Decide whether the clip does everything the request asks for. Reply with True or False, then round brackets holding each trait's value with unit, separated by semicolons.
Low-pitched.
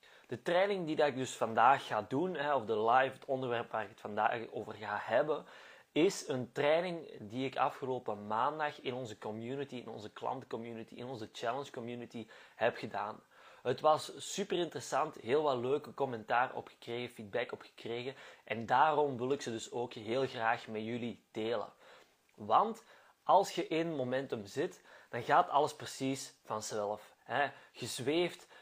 True (125 Hz)